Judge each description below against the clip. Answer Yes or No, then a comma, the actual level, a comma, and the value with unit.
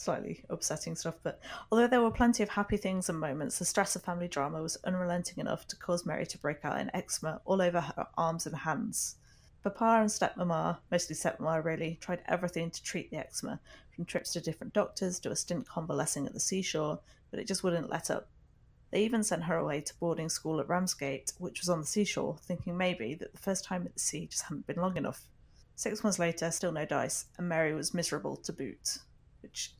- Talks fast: Yes, fast, 215 wpm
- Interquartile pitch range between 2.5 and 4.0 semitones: Yes, average, 2.9 semitones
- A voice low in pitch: No, medium, 175 Hz